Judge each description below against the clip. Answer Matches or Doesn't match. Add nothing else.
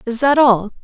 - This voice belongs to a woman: Matches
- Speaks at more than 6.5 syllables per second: Doesn't match